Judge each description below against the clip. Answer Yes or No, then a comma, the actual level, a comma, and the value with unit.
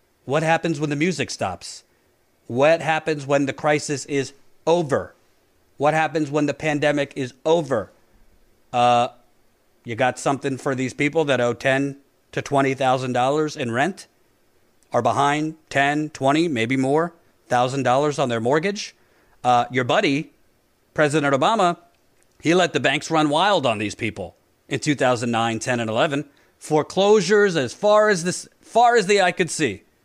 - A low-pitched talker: No, medium, 145 Hz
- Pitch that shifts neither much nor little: Yes, average, 3.7 semitones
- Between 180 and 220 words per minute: No, average, 145 wpm